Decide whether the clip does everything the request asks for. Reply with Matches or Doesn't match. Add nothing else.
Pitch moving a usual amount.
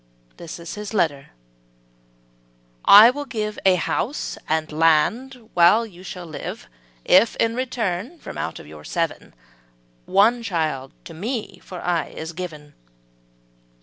Doesn't match